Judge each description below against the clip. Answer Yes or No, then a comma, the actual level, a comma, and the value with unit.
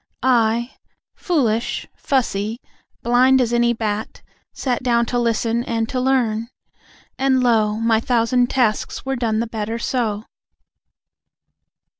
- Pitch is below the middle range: No, high, 235 Hz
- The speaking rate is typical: No, slow, 120 wpm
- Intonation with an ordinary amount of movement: No, narrow, 2.1 semitones